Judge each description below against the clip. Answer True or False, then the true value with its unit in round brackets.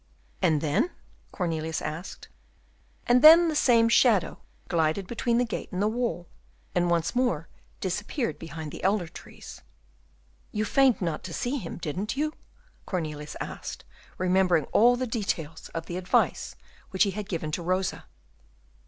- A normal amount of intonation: False (6.0 semitones)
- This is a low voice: False (185 Hz)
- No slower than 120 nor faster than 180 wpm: True (150 wpm)